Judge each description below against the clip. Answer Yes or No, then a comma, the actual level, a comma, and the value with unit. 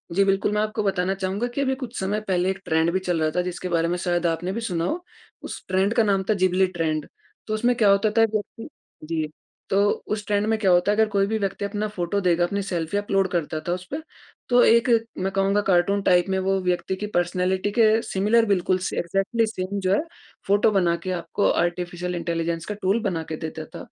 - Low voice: No, high, 190 Hz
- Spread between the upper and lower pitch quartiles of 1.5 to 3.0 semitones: Yes, average, 2.7 semitones